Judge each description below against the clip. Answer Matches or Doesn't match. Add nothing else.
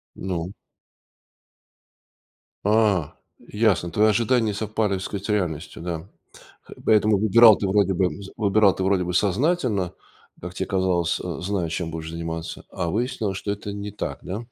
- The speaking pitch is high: Doesn't match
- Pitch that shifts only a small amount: Doesn't match